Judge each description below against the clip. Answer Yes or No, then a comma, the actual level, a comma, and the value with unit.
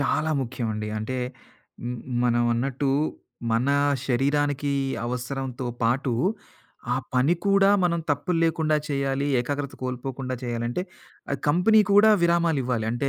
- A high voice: No, low, 135 Hz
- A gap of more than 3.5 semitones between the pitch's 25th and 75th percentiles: Yes, average, 3.9 semitones